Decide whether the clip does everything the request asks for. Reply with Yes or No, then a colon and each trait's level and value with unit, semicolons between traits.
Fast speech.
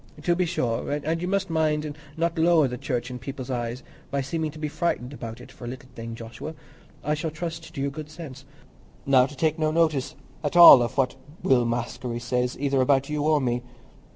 Yes: fast, 215 wpm